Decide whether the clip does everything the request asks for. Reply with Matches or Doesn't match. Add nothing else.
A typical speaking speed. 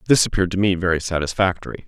Matches